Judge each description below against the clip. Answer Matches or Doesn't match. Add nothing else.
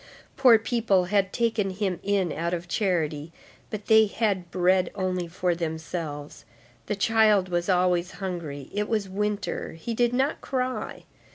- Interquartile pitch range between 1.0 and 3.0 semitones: Doesn't match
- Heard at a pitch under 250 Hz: Matches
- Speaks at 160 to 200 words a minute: Doesn't match